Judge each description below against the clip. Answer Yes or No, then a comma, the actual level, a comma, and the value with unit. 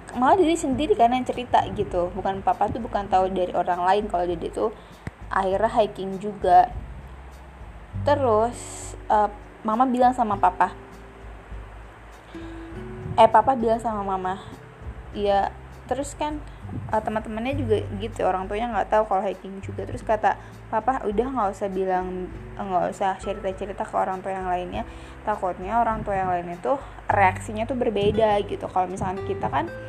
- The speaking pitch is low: No, high, 195 Hz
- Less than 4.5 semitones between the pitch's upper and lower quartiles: Yes, average, 3.9 semitones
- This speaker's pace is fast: Yes, fast, 155 wpm